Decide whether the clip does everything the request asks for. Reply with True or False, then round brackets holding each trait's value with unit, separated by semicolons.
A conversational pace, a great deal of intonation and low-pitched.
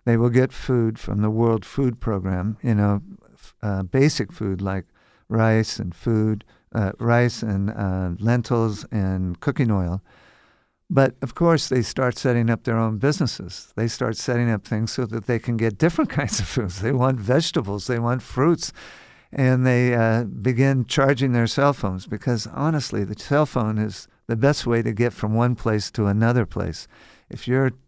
False (180 wpm; 3.2 semitones; 115 Hz)